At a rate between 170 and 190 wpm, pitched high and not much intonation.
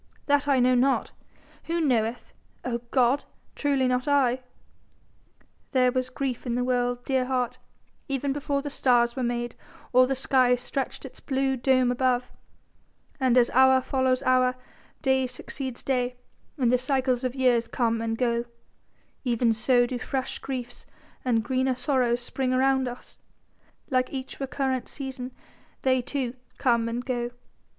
No: average, 150 wpm; very high, 255 Hz; narrow, 1.4 semitones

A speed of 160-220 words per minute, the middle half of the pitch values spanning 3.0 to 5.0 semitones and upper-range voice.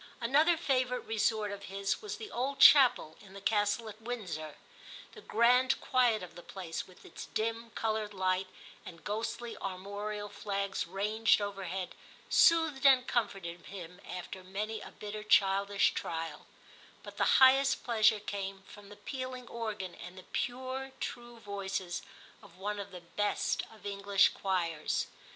No: average, 150 wpm; average, 3.8 semitones; high, 205 Hz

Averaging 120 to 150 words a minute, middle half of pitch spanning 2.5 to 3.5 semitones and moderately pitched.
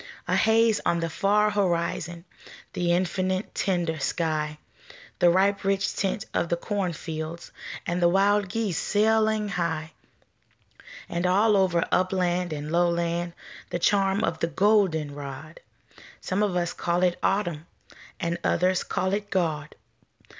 Yes: slow, 135 wpm; average, 2.8 semitones; medium, 180 Hz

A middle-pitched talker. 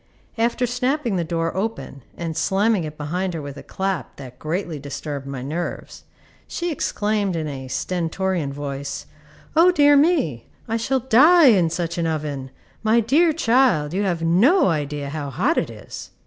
Yes: medium, 175 Hz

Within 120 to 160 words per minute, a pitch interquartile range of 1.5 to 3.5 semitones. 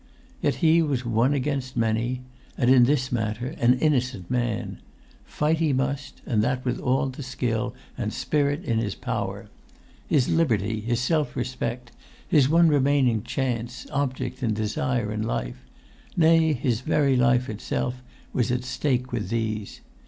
Yes: average, 150 wpm; average, 3.2 semitones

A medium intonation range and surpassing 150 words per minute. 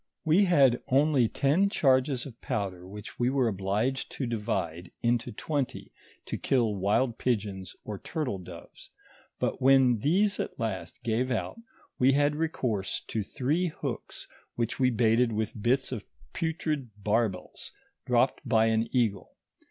No: average, 4.4 semitones; average, 145 wpm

